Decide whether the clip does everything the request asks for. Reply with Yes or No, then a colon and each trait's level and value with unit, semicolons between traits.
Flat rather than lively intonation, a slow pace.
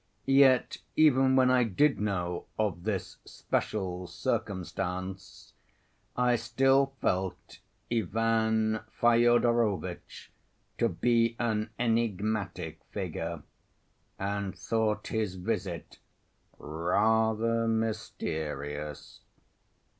No: average, 4.2 semitones; slow, 80 wpm